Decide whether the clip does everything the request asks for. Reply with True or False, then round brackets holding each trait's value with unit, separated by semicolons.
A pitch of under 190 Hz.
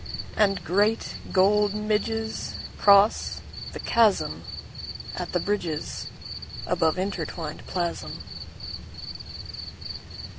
False (200 Hz)